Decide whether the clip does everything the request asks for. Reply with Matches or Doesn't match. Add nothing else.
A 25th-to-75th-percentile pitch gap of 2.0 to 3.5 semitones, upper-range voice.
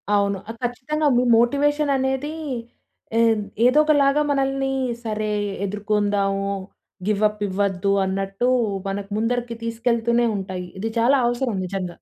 Doesn't match